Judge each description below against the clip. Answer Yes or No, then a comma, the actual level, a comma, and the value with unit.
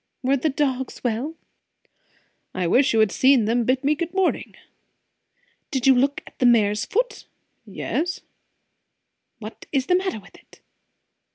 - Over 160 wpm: No, average, 150 wpm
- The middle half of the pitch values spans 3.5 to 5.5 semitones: Yes, average, 4.5 semitones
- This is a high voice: Yes, very high, 265 Hz